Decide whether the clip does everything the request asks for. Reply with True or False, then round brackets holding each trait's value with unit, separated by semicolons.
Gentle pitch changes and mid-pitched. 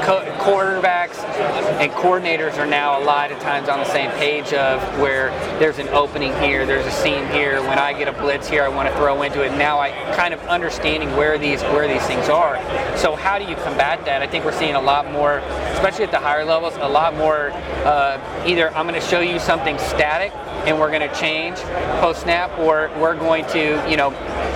True (2.3 semitones; 145 Hz)